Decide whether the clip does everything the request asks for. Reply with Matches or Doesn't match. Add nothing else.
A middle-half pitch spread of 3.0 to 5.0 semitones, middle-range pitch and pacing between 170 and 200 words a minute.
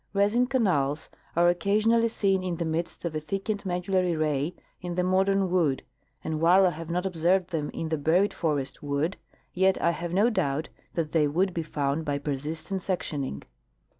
Matches